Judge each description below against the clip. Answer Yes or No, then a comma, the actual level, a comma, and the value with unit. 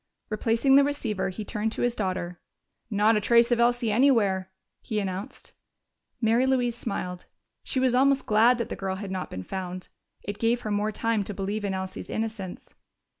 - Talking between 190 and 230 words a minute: No, average, 180 wpm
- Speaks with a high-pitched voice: Yes, high, 215 Hz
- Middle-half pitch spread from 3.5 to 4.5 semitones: Yes, average, 3.8 semitones